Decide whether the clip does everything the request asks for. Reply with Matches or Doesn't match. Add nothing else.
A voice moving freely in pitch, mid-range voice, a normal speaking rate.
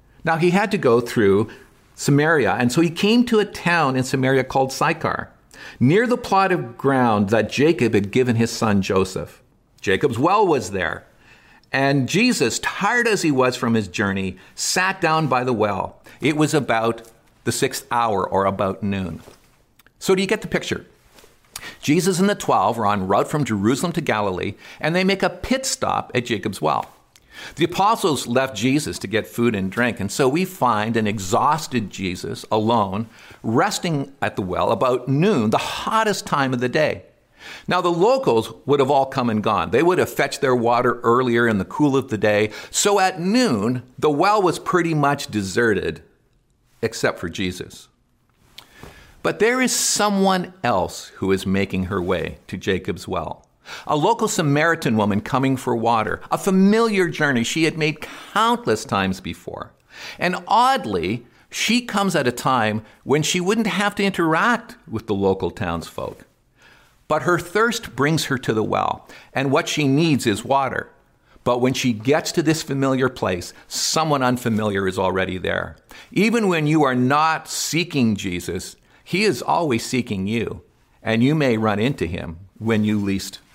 Doesn't match